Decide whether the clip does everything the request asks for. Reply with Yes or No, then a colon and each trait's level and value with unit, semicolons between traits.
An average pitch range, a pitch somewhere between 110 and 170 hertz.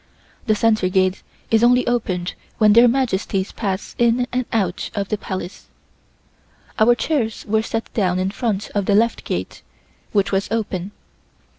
No: average, 3.2 semitones; high, 215 Hz